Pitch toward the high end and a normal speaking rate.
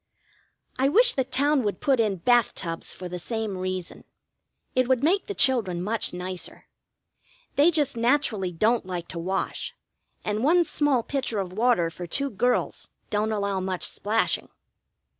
Yes: high, 220 Hz; average, 160 wpm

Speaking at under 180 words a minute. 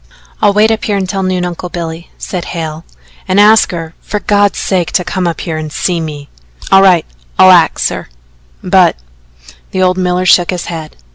No: average, 190 wpm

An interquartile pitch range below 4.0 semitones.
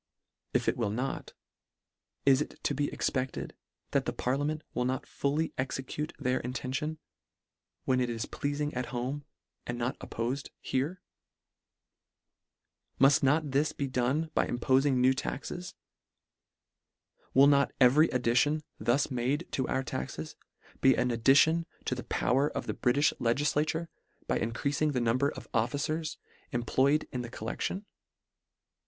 Yes: average, 2.8 semitones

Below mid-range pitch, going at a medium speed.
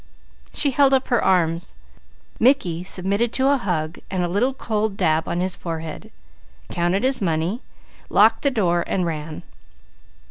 No: high, 190 Hz; average, 150 wpm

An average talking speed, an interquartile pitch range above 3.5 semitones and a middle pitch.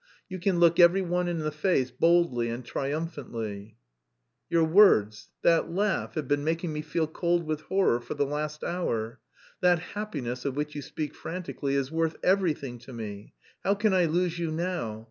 Yes: average, 180 wpm; average, 4.6 semitones; medium, 160 Hz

